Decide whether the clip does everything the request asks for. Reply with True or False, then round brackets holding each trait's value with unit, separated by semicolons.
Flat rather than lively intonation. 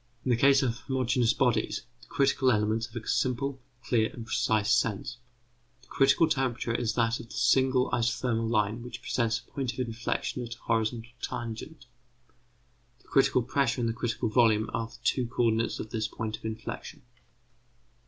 True (2.3 semitones)